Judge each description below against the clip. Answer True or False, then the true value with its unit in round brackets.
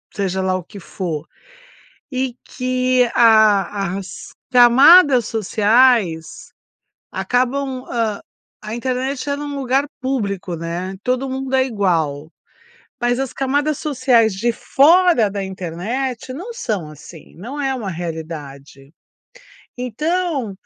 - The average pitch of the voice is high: True (235 Hz)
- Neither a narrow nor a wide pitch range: False (5.7 semitones)